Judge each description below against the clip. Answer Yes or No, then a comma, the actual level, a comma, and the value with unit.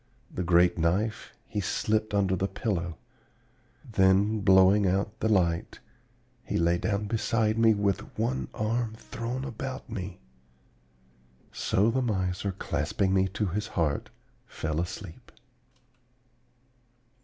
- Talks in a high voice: No, low, 100 Hz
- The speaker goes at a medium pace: No, slow, 120 wpm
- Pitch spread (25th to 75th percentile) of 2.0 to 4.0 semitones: Yes, average, 3.3 semitones